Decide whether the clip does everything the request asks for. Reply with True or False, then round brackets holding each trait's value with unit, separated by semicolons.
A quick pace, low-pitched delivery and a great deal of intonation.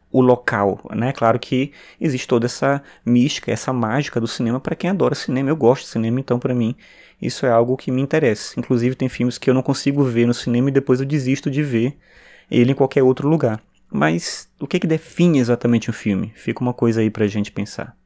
False (225 wpm; 125 Hz; 2.9 semitones)